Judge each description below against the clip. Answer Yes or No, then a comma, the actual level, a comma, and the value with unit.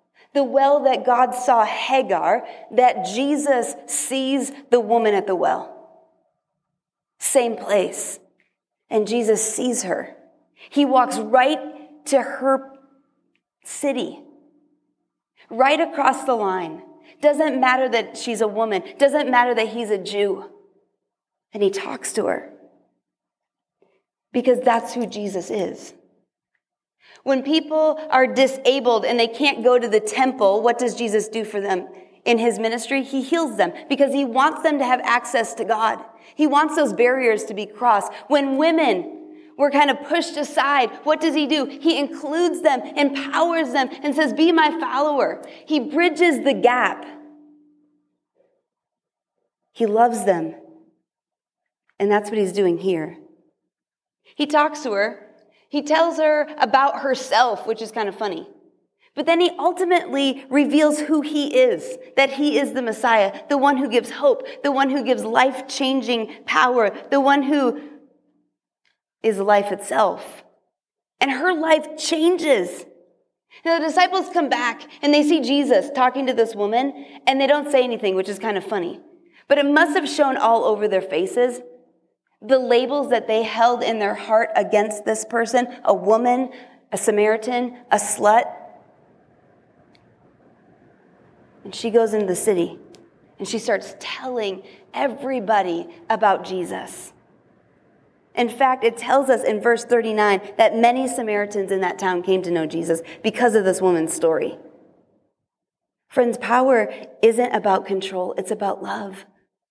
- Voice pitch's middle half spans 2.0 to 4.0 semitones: No, average, 4.9 semitones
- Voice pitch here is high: Yes, very high, 260 Hz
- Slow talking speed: No, average, 145 wpm